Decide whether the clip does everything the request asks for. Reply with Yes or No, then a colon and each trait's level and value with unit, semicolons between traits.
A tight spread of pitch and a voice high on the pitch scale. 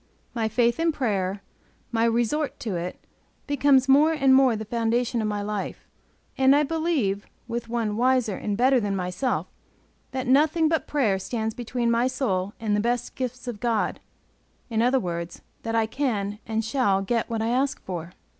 No: average, 4.0 semitones; high, 235 Hz